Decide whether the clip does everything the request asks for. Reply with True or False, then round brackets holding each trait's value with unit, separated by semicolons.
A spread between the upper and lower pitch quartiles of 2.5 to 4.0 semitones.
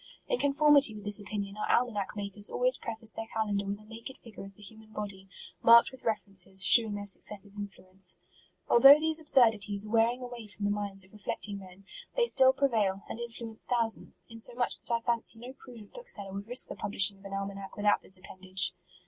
True (3.0 semitones)